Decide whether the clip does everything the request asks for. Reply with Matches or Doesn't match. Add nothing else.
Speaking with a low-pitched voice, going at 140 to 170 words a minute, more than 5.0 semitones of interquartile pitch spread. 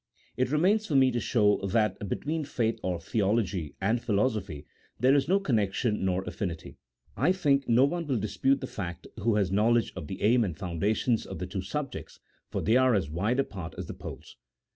Doesn't match